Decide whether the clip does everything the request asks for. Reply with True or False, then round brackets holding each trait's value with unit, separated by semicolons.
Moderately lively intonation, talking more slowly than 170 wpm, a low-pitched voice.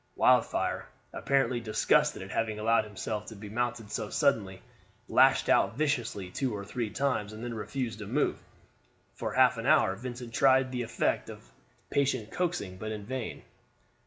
True (3.5 semitones; 160 wpm; 115 Hz)